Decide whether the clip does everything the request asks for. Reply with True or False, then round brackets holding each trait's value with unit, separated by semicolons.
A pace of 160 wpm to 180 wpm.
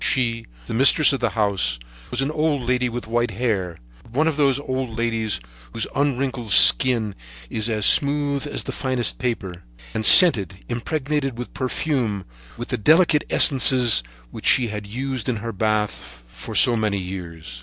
True (165 wpm)